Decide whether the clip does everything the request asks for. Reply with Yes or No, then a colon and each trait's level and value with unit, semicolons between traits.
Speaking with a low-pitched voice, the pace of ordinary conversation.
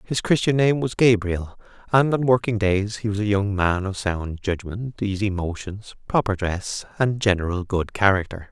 Yes: low, 105 Hz; average, 175 wpm